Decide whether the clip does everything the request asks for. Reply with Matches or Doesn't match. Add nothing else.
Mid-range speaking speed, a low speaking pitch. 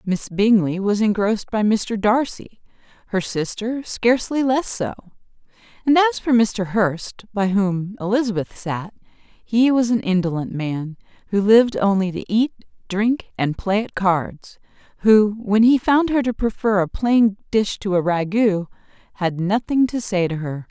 Doesn't match